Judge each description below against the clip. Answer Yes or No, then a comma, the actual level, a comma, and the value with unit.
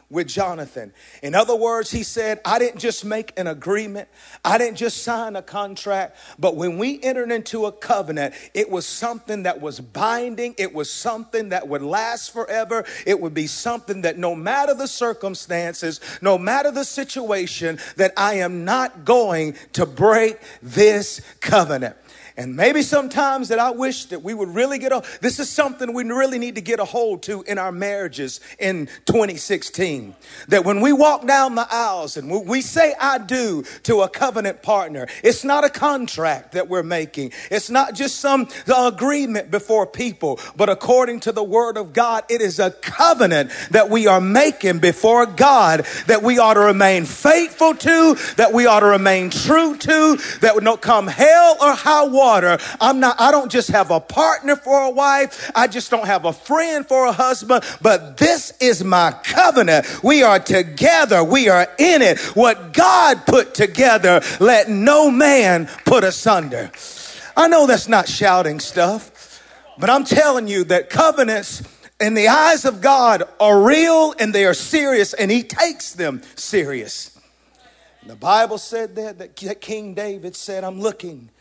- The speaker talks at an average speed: Yes, average, 175 wpm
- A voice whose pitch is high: Yes, high, 220 Hz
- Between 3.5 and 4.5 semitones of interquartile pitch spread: No, wide, 5.4 semitones